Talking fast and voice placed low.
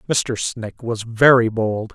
No: average, 155 wpm; low, 115 Hz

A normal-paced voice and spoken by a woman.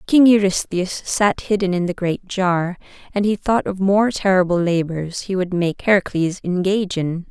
Yes: average, 175 wpm; female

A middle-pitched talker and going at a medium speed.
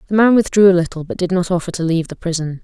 No: medium, 180 Hz; fast, 295 wpm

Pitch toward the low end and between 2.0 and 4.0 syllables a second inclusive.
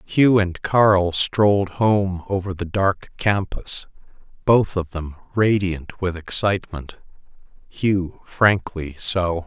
Yes: very low, 95 Hz; 3.3 syllables/s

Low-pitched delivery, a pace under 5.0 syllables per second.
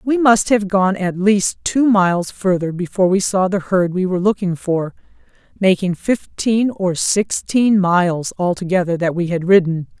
No: high, 190 Hz; 4.6 syllables/s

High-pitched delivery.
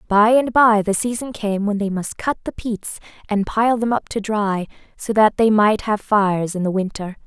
Yes: high, 210 Hz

